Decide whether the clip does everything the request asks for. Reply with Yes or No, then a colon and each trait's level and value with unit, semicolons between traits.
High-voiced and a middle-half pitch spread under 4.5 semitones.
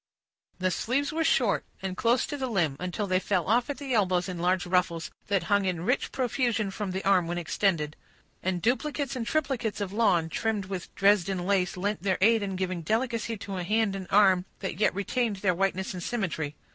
Yes: high, 195 Hz; average, 3.7 semitones